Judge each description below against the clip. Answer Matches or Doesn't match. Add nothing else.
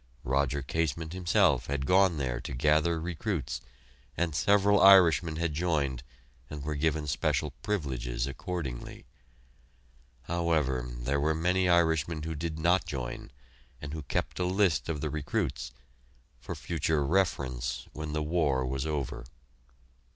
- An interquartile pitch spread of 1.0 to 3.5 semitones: Doesn't match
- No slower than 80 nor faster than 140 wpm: Matches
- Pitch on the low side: Matches